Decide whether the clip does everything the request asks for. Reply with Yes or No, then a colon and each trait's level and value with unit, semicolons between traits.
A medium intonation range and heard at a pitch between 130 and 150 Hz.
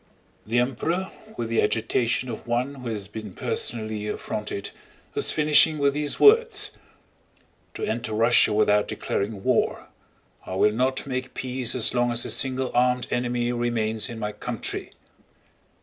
No: average, 3.0 semitones; low, 120 Hz